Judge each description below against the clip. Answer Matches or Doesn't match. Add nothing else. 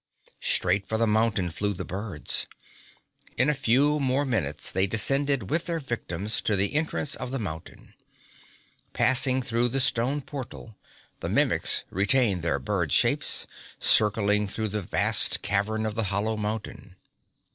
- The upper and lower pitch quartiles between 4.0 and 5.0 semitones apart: Matches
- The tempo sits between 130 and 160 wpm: Matches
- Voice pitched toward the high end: Doesn't match